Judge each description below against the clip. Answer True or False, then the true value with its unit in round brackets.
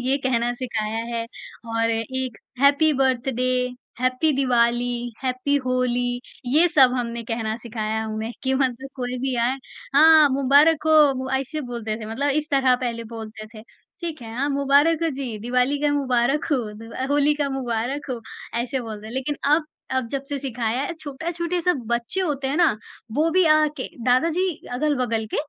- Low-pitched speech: False (255 Hz)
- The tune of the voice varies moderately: True (3.3 semitones)